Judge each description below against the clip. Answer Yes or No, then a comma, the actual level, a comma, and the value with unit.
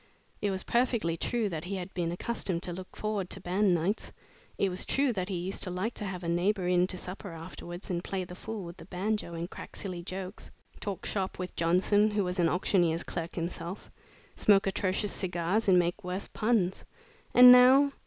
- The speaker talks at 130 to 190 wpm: No, fast, 205 wpm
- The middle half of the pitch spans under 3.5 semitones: Yes, average, 2.8 semitones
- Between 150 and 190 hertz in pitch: Yes, medium, 185 Hz